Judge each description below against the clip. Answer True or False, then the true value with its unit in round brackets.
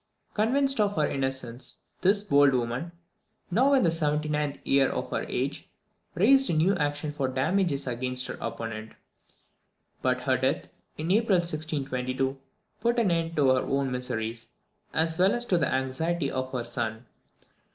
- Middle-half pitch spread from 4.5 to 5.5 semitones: True (5.1 semitones)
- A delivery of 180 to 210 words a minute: False (155 wpm)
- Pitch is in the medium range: True (145 Hz)